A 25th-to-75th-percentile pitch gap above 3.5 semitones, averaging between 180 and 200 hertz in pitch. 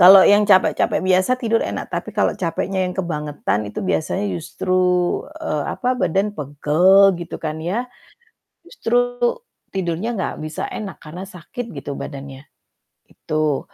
Yes: average, 4.4 semitones; medium, 185 Hz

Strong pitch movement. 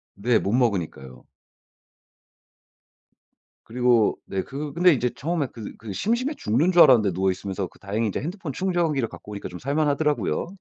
Yes: wide, 7.6 semitones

